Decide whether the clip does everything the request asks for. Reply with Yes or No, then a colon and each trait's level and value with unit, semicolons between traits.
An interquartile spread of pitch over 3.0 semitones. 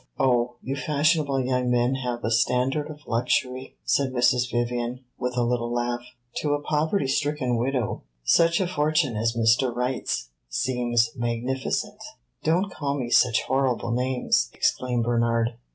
No: narrow, 2.4 semitones